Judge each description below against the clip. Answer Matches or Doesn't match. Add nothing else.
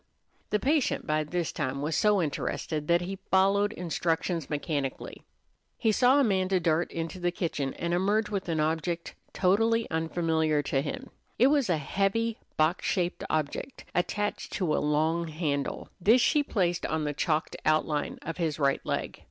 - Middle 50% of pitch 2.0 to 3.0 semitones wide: Doesn't match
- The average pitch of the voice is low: Doesn't match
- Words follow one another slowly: Doesn't match